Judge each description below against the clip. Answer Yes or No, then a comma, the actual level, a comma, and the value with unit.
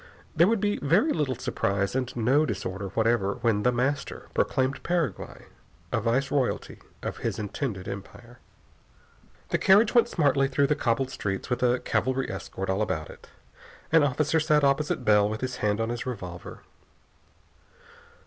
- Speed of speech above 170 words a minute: No, average, 155 wpm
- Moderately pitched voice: No, low, 125 Hz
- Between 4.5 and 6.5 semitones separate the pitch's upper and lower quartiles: Yes, average, 5.2 semitones